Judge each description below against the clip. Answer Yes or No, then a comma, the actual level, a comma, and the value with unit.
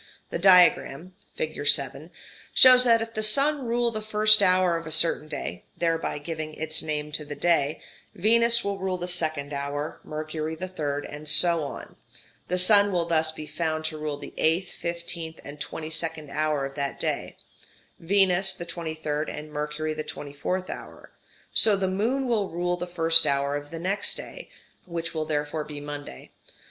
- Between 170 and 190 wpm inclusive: Yes, average, 180 wpm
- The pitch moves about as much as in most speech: Yes, average, 3.6 semitones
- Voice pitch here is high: No, medium, 165 Hz